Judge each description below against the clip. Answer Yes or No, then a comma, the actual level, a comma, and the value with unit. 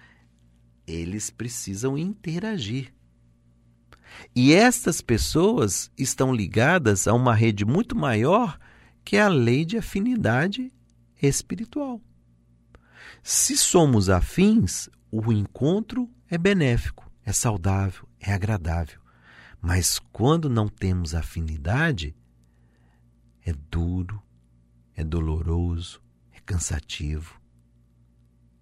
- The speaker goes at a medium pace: No, slow, 90 wpm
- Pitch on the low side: Yes, very low, 95 Hz